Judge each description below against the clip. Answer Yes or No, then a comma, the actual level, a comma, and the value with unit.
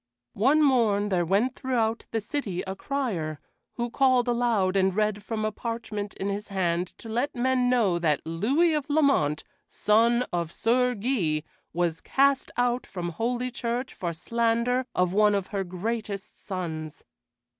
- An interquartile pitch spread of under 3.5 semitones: No, average, 4.9 semitones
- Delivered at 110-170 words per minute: Yes, average, 155 wpm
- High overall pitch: Yes, high, 220 Hz